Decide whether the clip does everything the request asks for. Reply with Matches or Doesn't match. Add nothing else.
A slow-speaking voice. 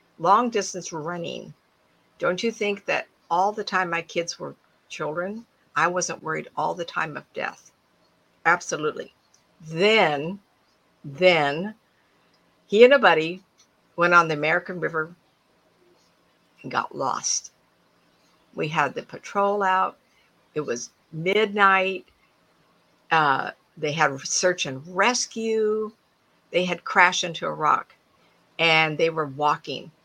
Matches